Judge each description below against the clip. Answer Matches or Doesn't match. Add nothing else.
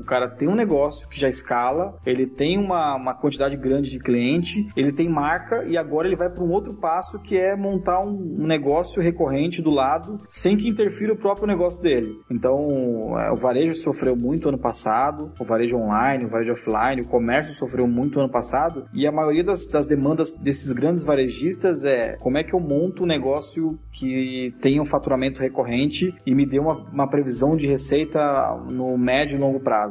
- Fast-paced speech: Matches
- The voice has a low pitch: Doesn't match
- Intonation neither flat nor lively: Matches